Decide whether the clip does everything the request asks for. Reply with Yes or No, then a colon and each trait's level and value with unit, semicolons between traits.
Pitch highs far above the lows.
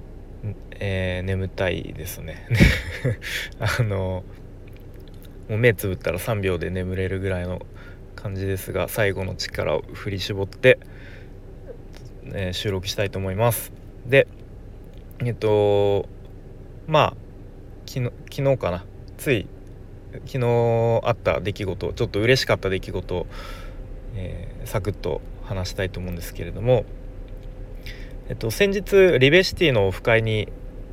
No: average, 3.3 semitones